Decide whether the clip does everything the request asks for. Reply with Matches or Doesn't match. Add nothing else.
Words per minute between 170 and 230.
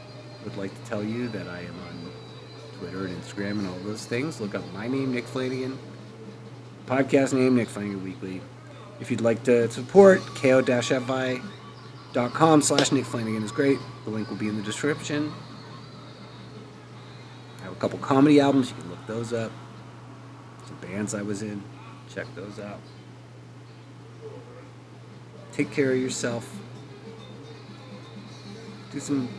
Doesn't match